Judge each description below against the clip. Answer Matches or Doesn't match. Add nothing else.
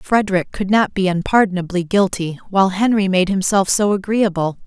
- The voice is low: Doesn't match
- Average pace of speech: Matches